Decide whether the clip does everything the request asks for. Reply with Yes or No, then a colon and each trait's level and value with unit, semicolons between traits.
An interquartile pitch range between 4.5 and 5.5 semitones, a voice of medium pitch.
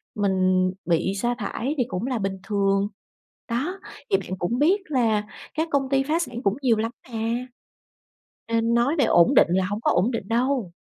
No: average, 5.1 semitones; high, 230 Hz